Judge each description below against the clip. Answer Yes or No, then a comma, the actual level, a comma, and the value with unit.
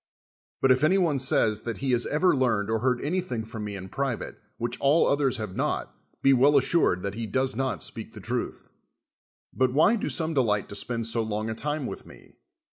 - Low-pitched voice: Yes, low, 125 Hz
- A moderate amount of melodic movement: Yes, average, 4.2 semitones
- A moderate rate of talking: No, fast, 215 wpm